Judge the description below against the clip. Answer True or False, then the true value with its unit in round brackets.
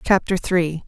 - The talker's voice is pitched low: False (175 Hz)